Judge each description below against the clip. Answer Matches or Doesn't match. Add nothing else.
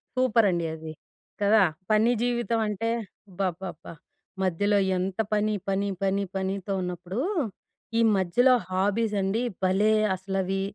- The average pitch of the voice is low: Doesn't match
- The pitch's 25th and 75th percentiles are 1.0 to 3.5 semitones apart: Matches